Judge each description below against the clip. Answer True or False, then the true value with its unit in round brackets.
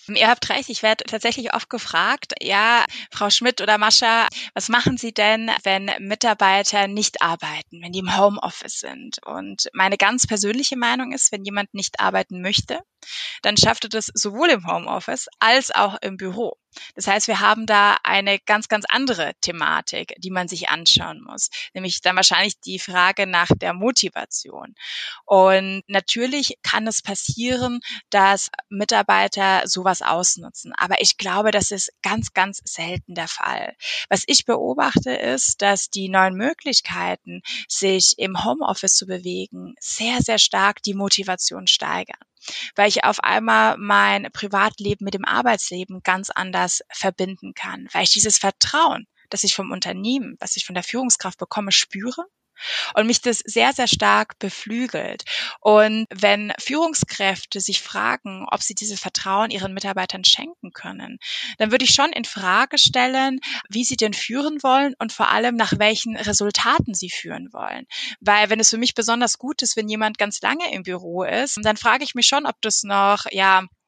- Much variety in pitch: False (3.6 semitones)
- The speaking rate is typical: True (165 wpm)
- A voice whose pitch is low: False (205 Hz)